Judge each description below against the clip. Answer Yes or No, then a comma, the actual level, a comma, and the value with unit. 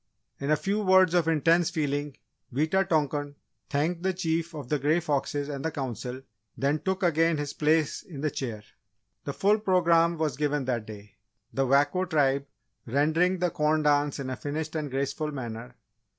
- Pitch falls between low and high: Yes, medium, 150 Hz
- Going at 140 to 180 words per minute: Yes, average, 175 wpm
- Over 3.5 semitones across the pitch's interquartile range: No, average, 3.2 semitones